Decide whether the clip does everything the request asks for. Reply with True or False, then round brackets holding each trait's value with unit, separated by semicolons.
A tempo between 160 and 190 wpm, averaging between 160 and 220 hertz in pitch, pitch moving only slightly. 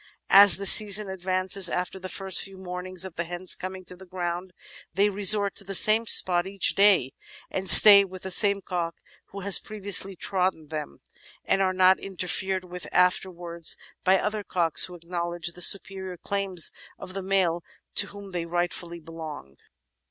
True (175 wpm; 185 Hz; 1.9 semitones)